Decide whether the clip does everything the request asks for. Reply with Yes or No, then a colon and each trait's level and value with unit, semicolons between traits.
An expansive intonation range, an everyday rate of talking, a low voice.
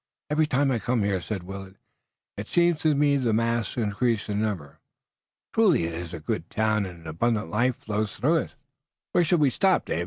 No: wide, 6.4 semitones; fast, 210 wpm; low, 110 Hz